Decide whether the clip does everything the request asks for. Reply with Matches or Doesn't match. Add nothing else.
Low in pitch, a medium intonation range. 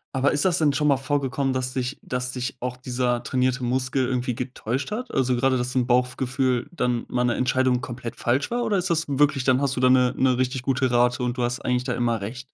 Doesn't match